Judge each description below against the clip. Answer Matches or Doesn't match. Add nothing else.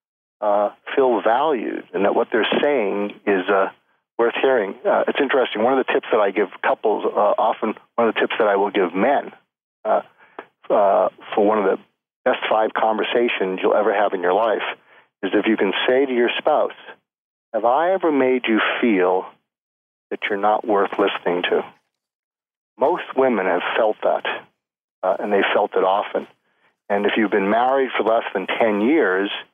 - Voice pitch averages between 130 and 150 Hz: Doesn't match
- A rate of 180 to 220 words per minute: Matches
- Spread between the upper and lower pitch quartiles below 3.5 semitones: Doesn't match